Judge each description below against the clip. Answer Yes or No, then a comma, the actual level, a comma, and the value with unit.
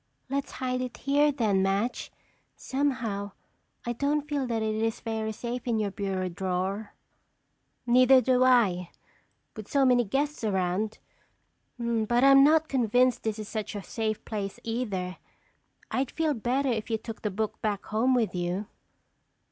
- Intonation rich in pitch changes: No, average, 3.8 semitones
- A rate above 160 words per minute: No, average, 155 wpm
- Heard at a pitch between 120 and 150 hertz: No, high, 225 Hz